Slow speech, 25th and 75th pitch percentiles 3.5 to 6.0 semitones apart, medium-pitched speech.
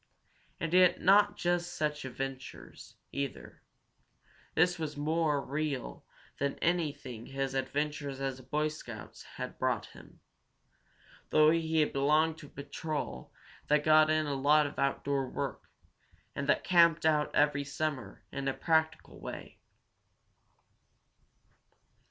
No: slow, 125 wpm; narrow, 2.5 semitones; medium, 150 Hz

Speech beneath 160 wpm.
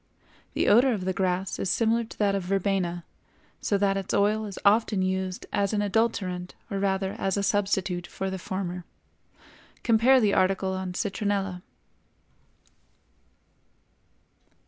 Yes: average, 140 wpm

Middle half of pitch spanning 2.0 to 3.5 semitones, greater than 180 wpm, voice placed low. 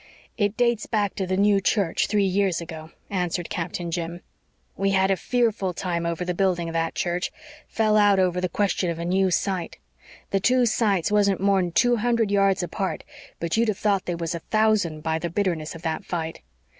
No: average, 3.2 semitones; average, 200 wpm; high, 190 Hz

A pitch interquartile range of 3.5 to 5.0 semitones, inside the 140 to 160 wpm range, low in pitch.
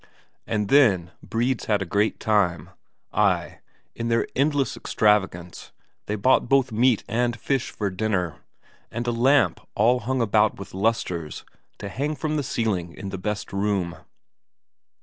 Yes: average, 3.9 semitones; average, 150 wpm; low, 110 Hz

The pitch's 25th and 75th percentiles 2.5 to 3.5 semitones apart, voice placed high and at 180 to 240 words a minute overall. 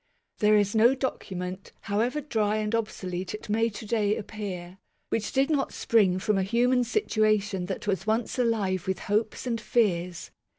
No: average, 3.1 semitones; high, 215 Hz; average, 165 wpm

